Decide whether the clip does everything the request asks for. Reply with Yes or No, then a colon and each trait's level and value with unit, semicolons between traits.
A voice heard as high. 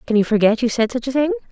Yes: high, 230 Hz